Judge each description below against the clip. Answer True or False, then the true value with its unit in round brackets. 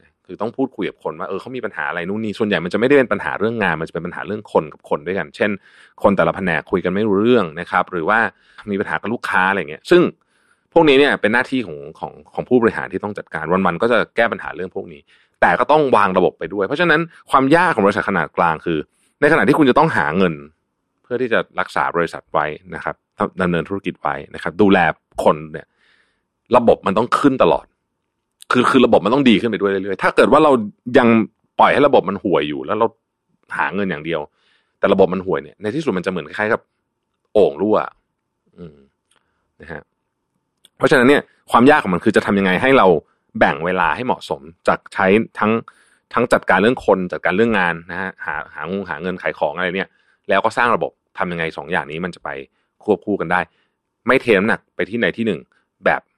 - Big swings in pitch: False (5.0 semitones)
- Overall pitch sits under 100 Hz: True (90 Hz)